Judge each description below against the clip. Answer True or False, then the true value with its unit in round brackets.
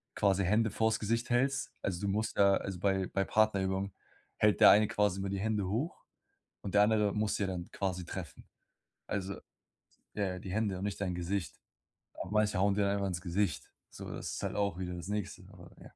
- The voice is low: True (100 Hz)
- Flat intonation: True (1.9 semitones)